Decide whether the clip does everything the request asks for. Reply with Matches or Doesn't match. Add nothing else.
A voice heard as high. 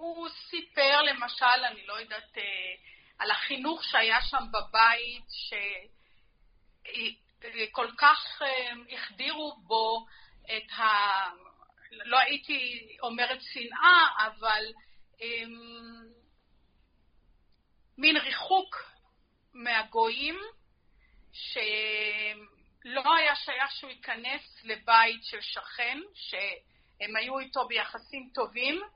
Matches